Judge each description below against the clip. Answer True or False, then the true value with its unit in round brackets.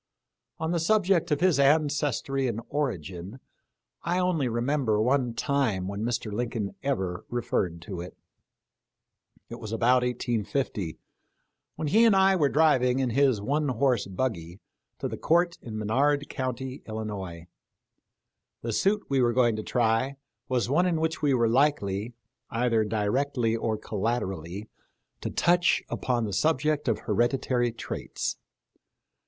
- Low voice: True (125 Hz)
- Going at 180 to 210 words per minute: False (140 wpm)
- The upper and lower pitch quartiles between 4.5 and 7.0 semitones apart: True (4.9 semitones)